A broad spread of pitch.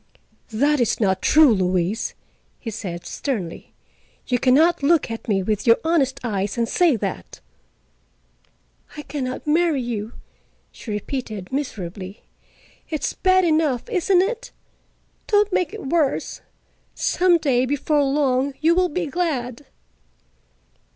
Yes: wide, 6.6 semitones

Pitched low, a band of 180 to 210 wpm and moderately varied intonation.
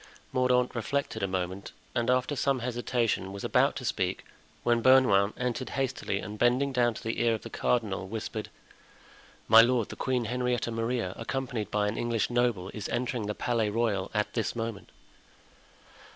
No: low, 115 Hz; average, 165 wpm; average, 3.0 semitones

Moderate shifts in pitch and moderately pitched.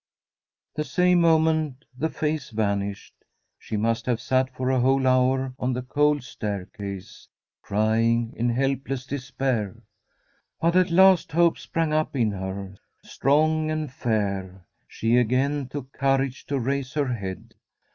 No: average, 4.7 semitones; low, 130 Hz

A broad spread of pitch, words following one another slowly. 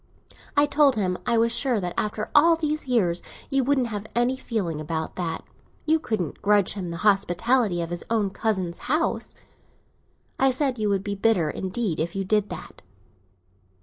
No: wide, 5.7 semitones; average, 175 wpm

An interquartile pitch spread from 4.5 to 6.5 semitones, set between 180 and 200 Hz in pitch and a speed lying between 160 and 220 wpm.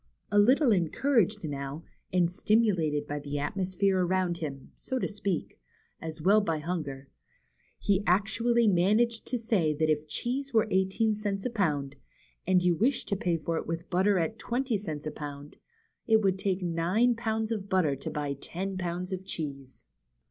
Yes: average, 5.2 semitones; medium, 185 Hz; average, 175 wpm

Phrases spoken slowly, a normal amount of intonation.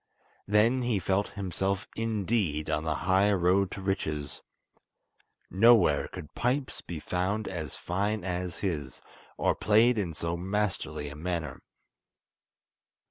Yes: slow, 125 wpm; average, 4.0 semitones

